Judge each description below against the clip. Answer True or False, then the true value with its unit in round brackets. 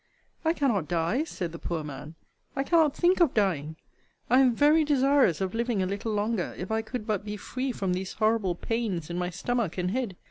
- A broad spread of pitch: True (6.1 semitones)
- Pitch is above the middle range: True (215 Hz)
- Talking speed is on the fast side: True (210 wpm)